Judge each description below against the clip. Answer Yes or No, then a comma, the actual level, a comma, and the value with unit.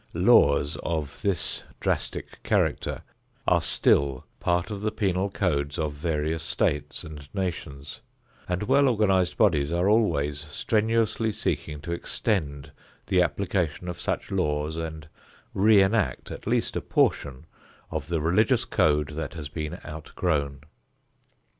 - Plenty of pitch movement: No, average, 4.7 semitones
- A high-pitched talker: No, very low, 80 Hz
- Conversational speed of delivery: No, slow, 130 wpm